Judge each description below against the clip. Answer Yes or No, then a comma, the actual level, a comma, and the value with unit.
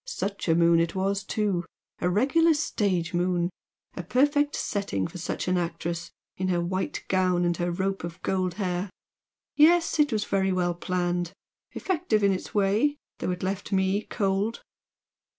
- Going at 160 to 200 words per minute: Yes, average, 165 wpm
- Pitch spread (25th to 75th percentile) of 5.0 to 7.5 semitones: No, average, 2.8 semitones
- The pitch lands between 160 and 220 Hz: Yes, high, 190 Hz